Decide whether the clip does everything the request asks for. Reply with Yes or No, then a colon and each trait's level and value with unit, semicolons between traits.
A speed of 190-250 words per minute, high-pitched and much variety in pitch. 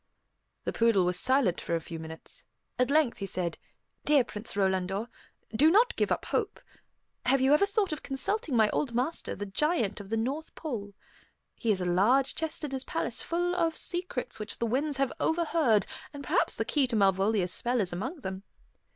Yes: average, 195 wpm; high, 245 Hz; wide, 7.3 semitones